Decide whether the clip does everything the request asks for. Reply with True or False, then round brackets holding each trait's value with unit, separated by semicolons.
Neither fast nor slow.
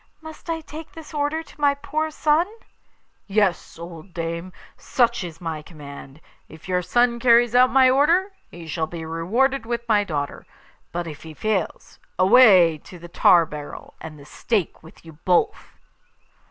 True (165 wpm)